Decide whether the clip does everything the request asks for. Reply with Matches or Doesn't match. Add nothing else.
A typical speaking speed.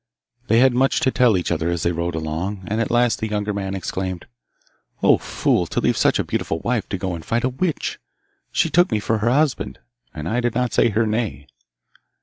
Doesn't match